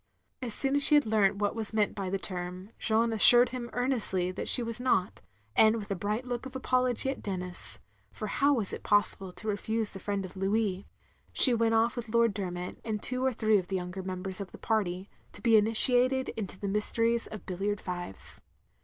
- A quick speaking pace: Yes, fast, 220 wpm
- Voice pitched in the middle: No, high, 215 Hz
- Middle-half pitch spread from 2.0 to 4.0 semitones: Yes, average, 3.5 semitones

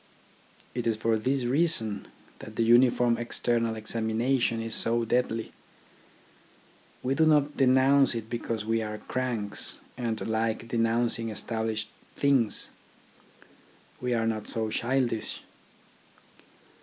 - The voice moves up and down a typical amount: No, narrow, 2.1 semitones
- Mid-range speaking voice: No, low, 115 Hz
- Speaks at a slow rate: Yes, slow, 115 wpm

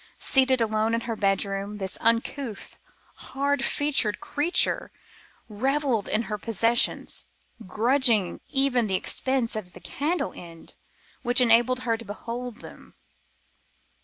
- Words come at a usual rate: No, slow, 120 wpm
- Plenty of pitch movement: No, average, 3.8 semitones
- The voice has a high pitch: Yes, high, 230 Hz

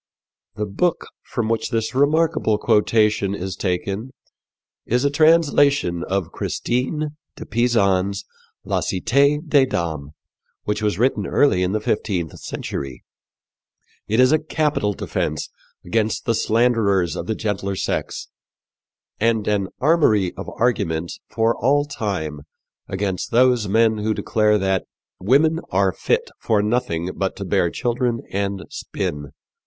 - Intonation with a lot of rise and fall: No, average, 4.6 semitones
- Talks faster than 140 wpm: No, slow, 135 wpm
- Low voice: Yes, low, 110 Hz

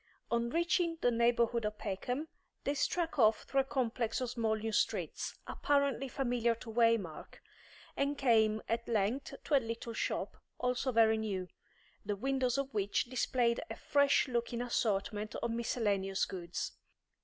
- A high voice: Yes, high, 235 Hz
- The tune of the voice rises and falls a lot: No, average, 3.1 semitones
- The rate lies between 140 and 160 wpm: Yes, average, 150 wpm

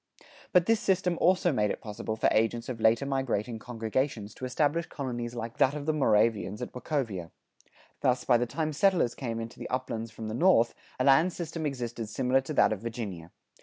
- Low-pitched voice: Yes, low, 125 Hz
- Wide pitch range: No, average, 4.5 semitones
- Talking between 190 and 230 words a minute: Yes, average, 200 wpm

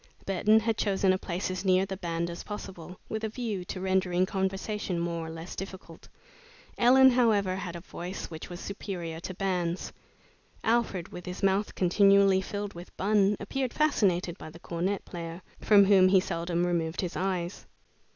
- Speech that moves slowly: No, average, 170 wpm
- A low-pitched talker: No, high, 190 Hz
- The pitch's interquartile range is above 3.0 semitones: No, narrow, 2.6 semitones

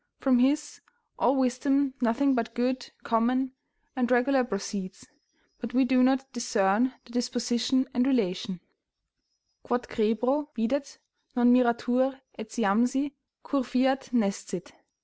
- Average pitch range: No, narrow, 2.2 semitones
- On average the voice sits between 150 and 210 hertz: No, high, 245 Hz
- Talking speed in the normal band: No, slow, 115 wpm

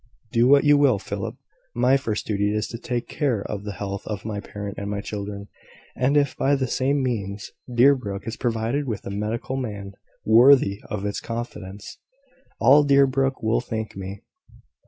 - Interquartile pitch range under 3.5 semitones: No, average, 4.4 semitones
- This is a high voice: No, low, 115 Hz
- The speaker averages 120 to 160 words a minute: No, average, 175 wpm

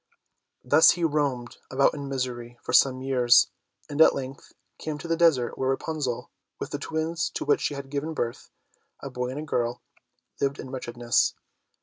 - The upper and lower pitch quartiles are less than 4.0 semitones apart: Yes, average, 3.3 semitones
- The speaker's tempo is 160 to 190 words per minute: Yes, average, 180 wpm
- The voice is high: No, low, 135 Hz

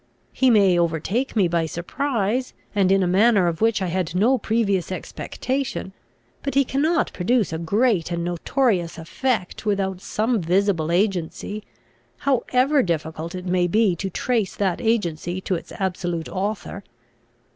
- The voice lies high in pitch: Yes, high, 195 Hz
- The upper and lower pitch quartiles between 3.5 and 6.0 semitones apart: Yes, average, 4.7 semitones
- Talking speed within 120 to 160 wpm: Yes, average, 145 wpm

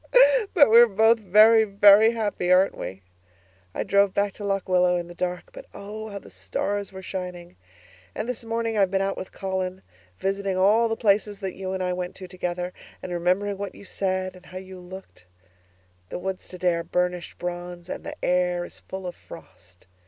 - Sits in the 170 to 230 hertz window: Yes, high, 190 Hz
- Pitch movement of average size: No, narrow, 2.2 semitones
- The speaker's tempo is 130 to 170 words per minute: No, average, 195 wpm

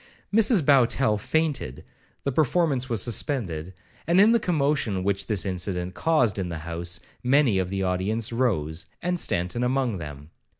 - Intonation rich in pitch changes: Yes, wide, 7.4 semitones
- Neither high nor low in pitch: No, low, 110 Hz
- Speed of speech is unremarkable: Yes, average, 155 wpm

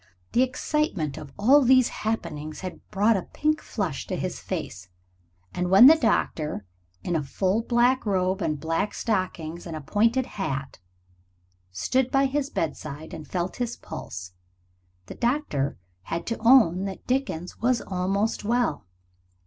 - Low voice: No, high, 195 Hz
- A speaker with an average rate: Yes, average, 150 wpm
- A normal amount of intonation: No, wide, 7.4 semitones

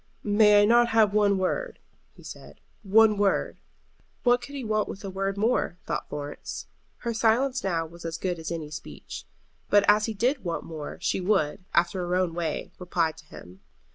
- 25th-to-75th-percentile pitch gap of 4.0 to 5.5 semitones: Yes, average, 4.5 semitones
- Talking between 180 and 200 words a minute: Yes, average, 190 wpm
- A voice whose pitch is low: No, high, 195 Hz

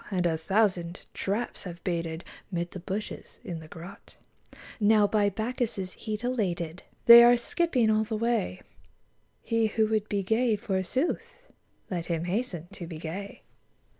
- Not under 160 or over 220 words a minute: No, average, 150 wpm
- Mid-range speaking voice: No, high, 200 Hz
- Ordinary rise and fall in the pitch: Yes, average, 4.3 semitones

